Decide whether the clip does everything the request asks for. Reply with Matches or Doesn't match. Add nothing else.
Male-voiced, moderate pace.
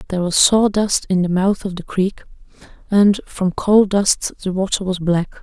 Doesn't match